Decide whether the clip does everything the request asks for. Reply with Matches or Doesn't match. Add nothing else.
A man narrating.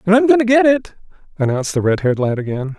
Matches